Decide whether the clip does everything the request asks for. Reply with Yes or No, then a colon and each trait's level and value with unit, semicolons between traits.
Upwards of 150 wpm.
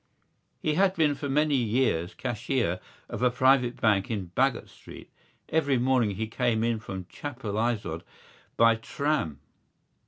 No: slow, 135 wpm